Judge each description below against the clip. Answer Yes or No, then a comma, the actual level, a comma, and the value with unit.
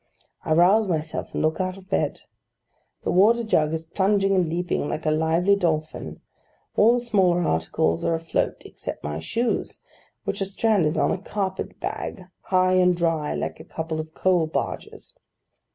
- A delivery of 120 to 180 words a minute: Yes, average, 170 wpm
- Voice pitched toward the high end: No, medium, 175 Hz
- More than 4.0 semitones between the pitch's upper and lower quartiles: No, average, 3.6 semitones